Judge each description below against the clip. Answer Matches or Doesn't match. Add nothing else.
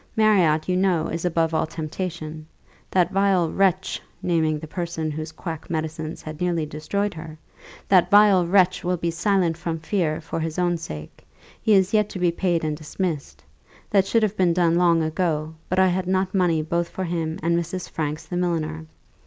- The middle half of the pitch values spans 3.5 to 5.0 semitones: Doesn't match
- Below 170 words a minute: Doesn't match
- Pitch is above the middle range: Doesn't match